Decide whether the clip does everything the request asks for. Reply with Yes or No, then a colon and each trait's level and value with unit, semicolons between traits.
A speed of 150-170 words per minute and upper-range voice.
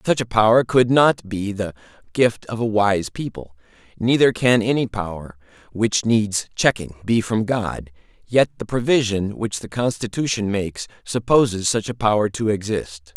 No: average, 160 wpm; low, 110 Hz